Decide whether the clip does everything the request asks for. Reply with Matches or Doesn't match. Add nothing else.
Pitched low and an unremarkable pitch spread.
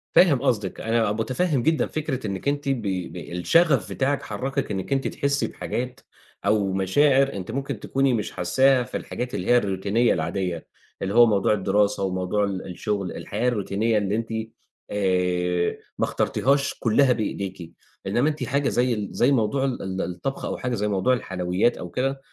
Doesn't match